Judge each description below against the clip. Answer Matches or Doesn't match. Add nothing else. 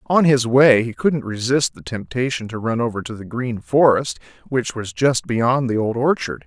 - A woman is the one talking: Doesn't match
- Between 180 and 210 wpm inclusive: Matches